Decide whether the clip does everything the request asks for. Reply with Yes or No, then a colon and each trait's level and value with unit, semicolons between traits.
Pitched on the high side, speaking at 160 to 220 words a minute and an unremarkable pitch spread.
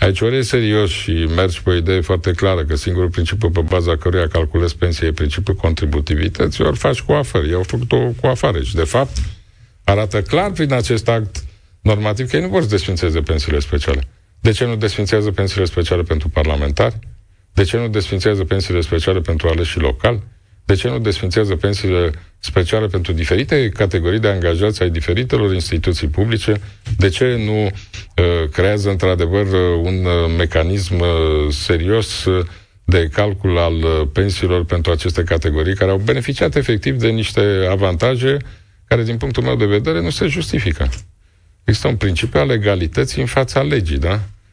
No: very low, 95 Hz; average, 165 wpm; average, 3.7 semitones